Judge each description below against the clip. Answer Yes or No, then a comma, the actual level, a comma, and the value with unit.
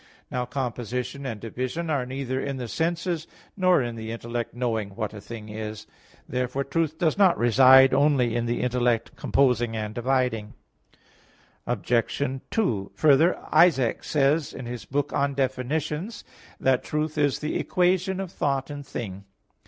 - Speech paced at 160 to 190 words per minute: No, average, 150 wpm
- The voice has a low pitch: Yes, low, 130 Hz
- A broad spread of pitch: No, average, 4.1 semitones